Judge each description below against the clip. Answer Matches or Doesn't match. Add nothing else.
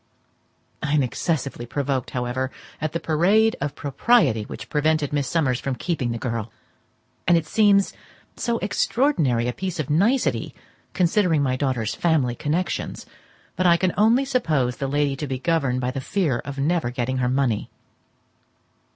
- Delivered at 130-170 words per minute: Matches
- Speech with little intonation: Doesn't match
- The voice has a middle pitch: Matches